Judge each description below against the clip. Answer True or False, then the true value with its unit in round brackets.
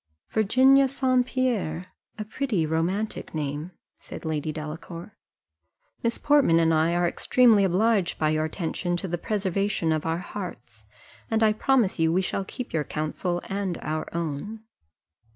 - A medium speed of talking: True (150 wpm)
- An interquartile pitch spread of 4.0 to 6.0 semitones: True (5.3 semitones)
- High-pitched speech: False (180 Hz)